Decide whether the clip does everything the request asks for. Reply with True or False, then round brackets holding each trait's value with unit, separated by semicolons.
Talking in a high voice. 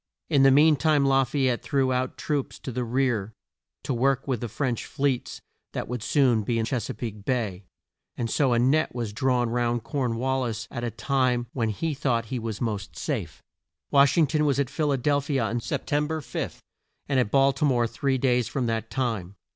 False (125 Hz)